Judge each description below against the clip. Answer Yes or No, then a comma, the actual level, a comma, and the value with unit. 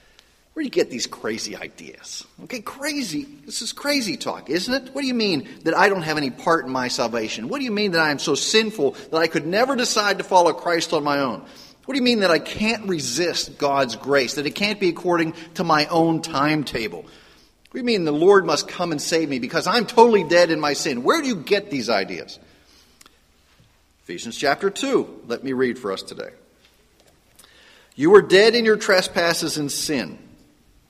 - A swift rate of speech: Yes, fast, 210 wpm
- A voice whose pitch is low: No, medium, 180 Hz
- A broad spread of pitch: Yes, wide, 7.3 semitones